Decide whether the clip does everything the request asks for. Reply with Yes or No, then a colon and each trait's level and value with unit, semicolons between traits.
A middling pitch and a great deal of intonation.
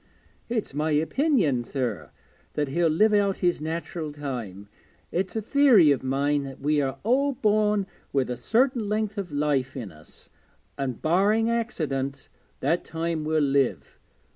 Yes: medium, 155 Hz; wide, 7.4 semitones